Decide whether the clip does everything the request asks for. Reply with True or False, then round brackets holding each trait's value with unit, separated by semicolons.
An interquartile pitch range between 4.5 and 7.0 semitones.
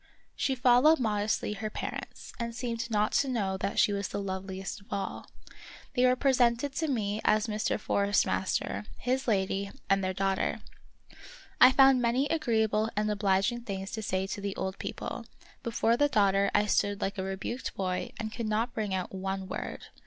False (3.5 semitones)